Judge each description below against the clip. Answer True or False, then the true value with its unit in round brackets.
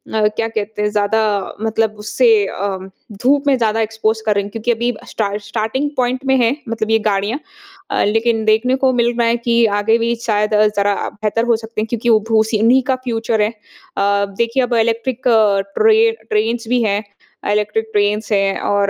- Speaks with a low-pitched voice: False (225 Hz)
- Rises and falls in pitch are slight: True (2.0 semitones)